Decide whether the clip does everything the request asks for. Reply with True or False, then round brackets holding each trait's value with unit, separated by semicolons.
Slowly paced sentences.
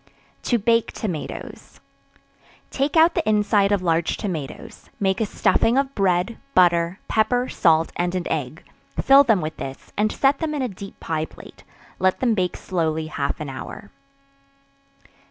False (155 wpm)